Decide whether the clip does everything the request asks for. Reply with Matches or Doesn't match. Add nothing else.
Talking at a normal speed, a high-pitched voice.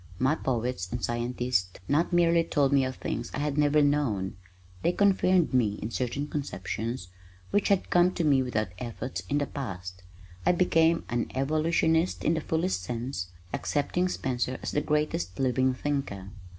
Doesn't match